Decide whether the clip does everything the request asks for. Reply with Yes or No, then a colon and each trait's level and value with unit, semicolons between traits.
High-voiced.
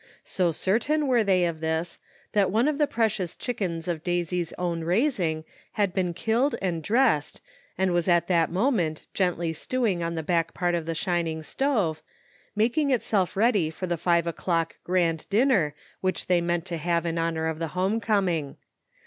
No: medium, 175 Hz